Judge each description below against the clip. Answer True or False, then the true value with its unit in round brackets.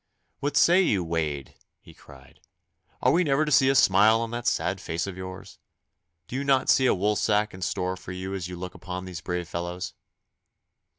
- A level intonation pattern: False (5.1 semitones)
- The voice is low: True (95 Hz)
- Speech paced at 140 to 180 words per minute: False (195 wpm)